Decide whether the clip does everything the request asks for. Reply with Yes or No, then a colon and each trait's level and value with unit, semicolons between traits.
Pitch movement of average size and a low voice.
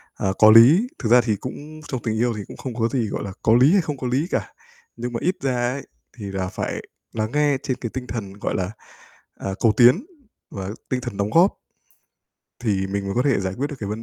Yes: average, 4.6 semitones; low, 120 Hz